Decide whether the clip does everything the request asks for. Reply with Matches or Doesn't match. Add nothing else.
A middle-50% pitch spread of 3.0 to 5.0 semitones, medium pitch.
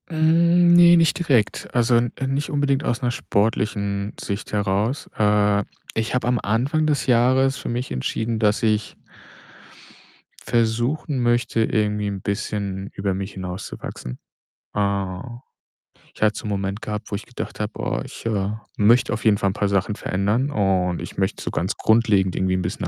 Doesn't match